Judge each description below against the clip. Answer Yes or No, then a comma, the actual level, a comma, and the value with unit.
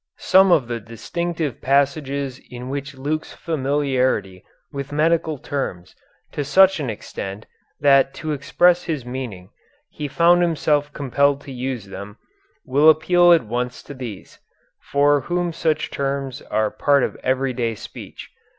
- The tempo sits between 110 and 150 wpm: Yes, average, 140 wpm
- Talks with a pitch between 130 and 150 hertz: Yes, medium, 140 Hz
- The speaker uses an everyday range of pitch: Yes, average, 3.7 semitones